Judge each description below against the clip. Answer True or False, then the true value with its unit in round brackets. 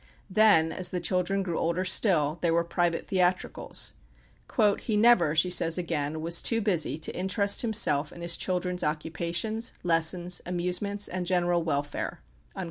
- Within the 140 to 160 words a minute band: True (145 wpm)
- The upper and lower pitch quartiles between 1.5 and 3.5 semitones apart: True (2.4 semitones)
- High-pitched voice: False (175 Hz)